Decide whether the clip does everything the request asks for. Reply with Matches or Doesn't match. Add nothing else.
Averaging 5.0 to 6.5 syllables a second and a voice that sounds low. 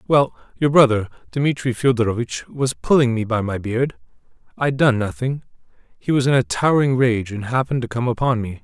Matches